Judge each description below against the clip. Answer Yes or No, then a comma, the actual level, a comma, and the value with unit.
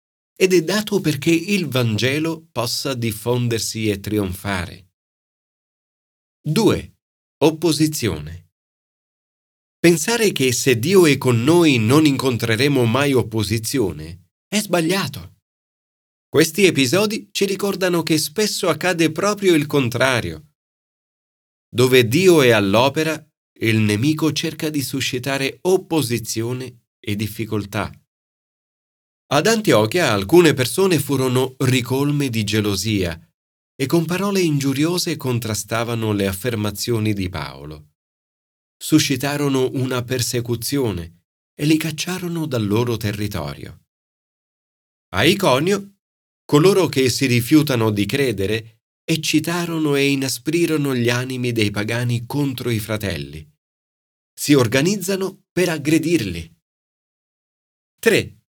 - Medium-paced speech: No, slow, 100 wpm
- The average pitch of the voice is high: No, low, 130 Hz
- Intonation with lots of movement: Yes, wide, 7.0 semitones